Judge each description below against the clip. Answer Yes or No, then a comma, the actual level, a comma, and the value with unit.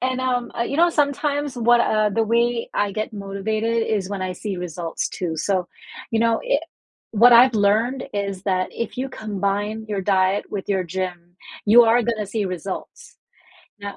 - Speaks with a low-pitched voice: No, high, 215 Hz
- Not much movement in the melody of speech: No, average, 3.4 semitones